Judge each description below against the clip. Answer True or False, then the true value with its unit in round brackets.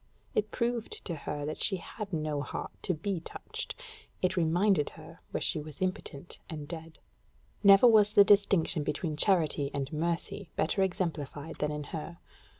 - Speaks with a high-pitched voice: False (165 Hz)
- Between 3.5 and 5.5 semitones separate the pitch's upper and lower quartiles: True (4.5 semitones)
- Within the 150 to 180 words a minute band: True (160 wpm)